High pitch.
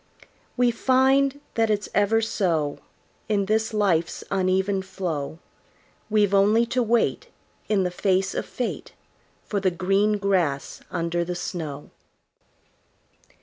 Yes: high, 195 Hz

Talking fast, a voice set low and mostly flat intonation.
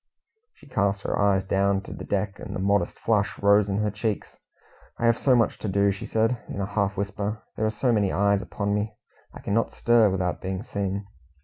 Yes: fast, 215 wpm; low, 100 Hz; narrow, 1.6 semitones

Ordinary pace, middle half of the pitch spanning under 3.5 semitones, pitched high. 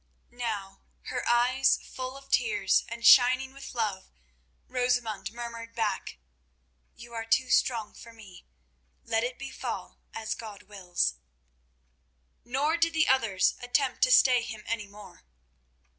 No: slow, 130 wpm; average, 2.9 semitones; high, 235 Hz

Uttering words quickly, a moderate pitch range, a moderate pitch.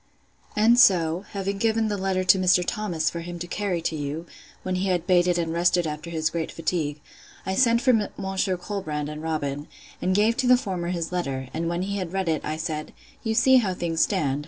Yes: fast, 215 wpm; average, 3.5 semitones; medium, 180 Hz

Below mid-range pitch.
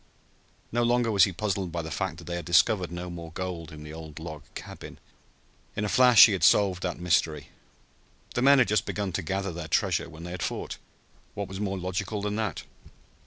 Yes: very low, 95 Hz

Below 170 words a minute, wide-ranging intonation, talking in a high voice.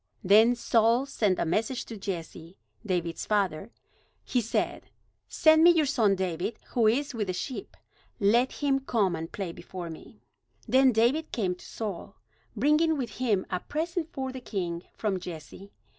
Yes: average, 160 wpm; wide, 6.0 semitones; high, 220 Hz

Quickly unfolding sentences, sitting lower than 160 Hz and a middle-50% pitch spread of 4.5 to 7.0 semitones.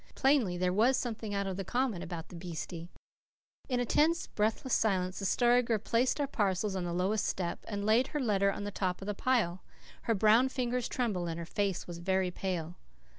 No: fast, 210 wpm; high, 205 Hz; average, 4.8 semitones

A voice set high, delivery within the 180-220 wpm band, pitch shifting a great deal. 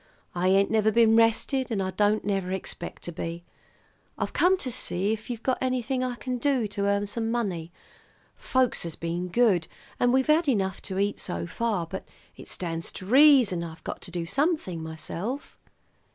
Yes: high, 205 Hz; average, 185 wpm; wide, 5.7 semitones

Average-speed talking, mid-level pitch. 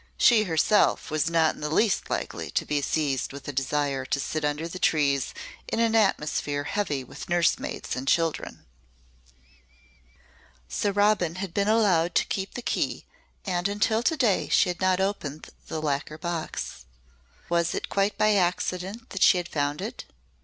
Yes: average, 165 wpm; medium, 170 Hz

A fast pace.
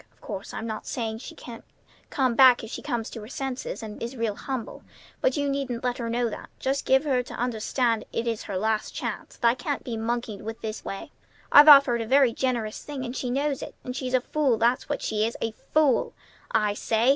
Yes: fast, 235 wpm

